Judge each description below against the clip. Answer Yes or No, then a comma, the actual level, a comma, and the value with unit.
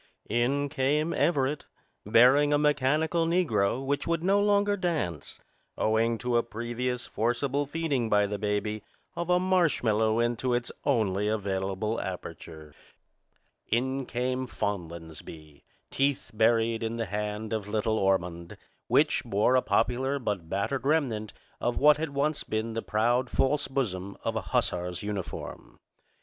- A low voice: Yes, low, 120 Hz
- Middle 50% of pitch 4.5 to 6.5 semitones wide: Yes, average, 5.2 semitones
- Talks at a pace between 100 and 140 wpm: Yes, slow, 135 wpm